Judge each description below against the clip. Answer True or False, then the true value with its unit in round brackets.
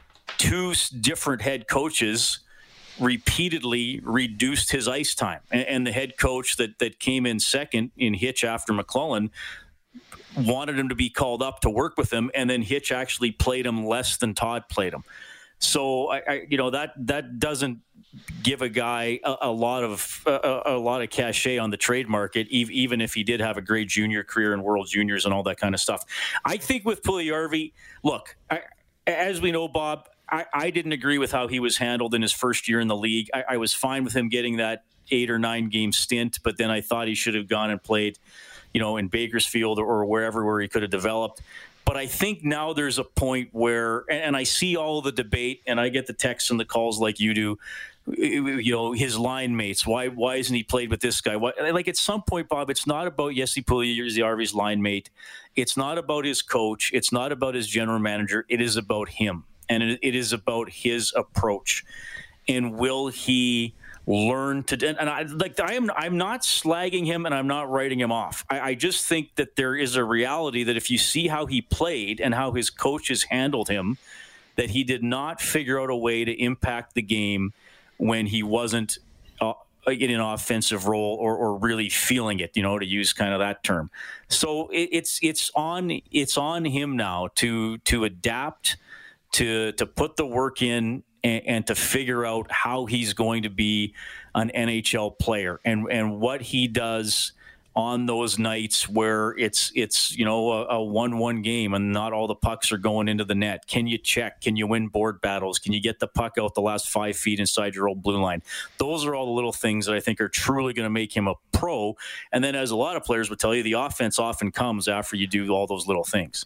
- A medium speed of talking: False (215 wpm)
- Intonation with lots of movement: False (3.3 semitones)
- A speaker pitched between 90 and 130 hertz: True (120 Hz)